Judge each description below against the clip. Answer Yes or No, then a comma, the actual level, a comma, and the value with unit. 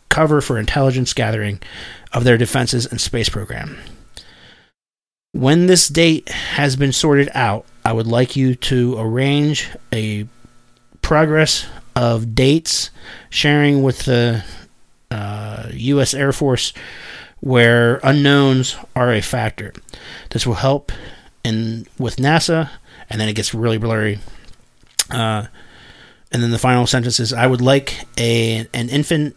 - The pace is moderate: No, slow, 130 wpm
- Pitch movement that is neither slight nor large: Yes, average, 3.3 semitones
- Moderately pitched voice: No, low, 120 Hz